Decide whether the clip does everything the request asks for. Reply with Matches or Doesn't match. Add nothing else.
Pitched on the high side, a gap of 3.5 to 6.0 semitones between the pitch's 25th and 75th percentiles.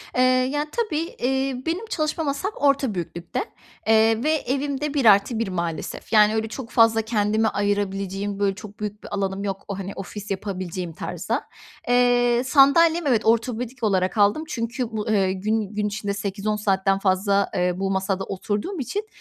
Matches